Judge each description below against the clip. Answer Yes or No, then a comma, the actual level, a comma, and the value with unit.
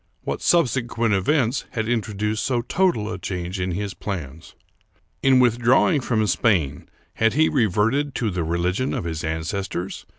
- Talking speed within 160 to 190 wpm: No, average, 145 wpm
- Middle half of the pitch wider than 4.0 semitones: Yes, wide, 5.5 semitones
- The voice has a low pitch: Yes, low, 105 Hz